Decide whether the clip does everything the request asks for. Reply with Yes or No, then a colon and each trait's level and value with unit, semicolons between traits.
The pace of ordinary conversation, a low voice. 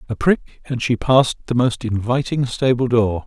Yes: average, 185 wpm; low, 120 Hz